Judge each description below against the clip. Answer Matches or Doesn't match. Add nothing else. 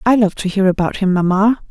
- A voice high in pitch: Matches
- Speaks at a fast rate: Matches